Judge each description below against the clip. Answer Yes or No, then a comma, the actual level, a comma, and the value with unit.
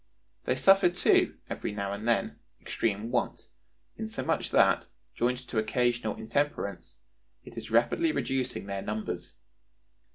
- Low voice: Yes, low, 115 Hz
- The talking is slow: Yes, slow, 125 wpm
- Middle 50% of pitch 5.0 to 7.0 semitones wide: No, average, 4.1 semitones